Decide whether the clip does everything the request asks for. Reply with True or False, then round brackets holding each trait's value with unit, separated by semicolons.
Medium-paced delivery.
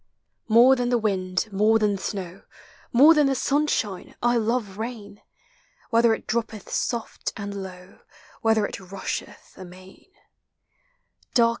False (130 wpm)